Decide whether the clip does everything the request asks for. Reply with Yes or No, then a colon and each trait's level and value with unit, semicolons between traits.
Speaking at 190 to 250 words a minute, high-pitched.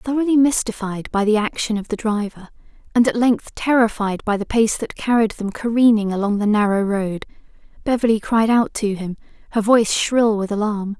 No: average, 180 wpm; high, 220 Hz